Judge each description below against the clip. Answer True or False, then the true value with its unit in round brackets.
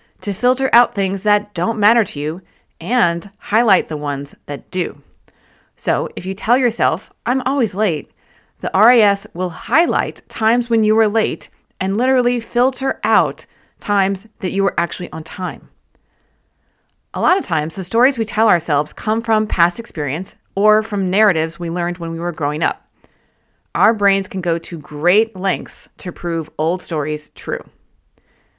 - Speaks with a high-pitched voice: True (195 Hz)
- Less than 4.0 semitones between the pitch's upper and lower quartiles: False (4.9 semitones)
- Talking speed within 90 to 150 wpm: False (165 wpm)